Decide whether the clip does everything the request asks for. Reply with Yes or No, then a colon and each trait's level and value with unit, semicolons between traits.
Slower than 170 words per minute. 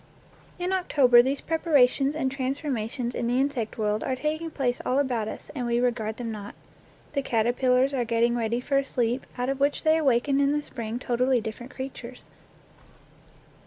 No: average, 180 wpm